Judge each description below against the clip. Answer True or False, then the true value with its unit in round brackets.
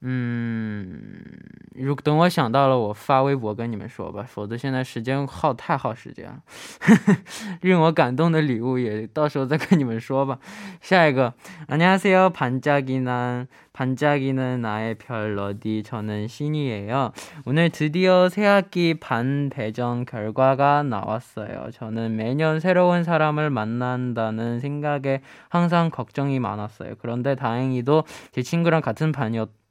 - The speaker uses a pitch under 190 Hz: True (135 Hz)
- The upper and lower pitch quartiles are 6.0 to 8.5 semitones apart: False (5.2 semitones)